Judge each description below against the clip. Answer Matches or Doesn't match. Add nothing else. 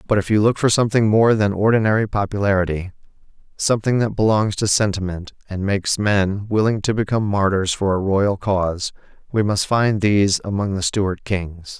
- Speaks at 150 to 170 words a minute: Matches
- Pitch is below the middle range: Matches